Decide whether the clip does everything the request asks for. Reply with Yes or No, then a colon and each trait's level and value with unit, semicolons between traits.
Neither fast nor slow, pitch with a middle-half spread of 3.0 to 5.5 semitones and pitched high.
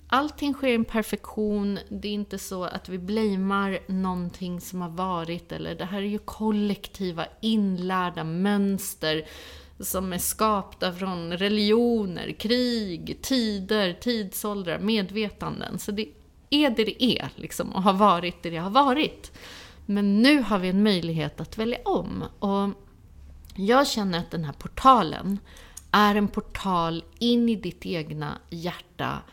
Yes: average, 145 wpm; average, 3.5 semitones; high, 200 Hz